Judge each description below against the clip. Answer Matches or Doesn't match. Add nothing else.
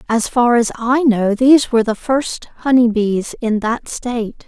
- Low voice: Doesn't match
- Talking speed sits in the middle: Matches